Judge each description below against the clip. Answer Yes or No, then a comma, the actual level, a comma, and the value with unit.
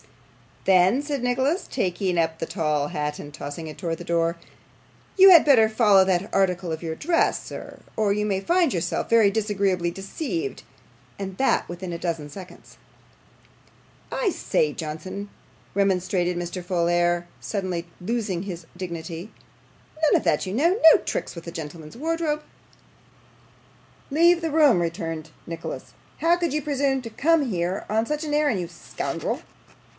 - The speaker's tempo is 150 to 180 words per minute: Yes, average, 155 wpm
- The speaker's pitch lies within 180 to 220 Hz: Yes, high, 190 Hz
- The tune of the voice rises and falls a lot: Yes, wide, 7.7 semitones